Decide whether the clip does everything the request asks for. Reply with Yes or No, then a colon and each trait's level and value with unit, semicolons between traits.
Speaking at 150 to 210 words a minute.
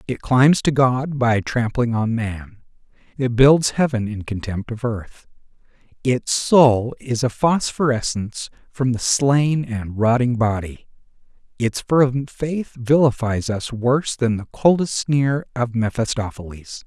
No: slow, 135 wpm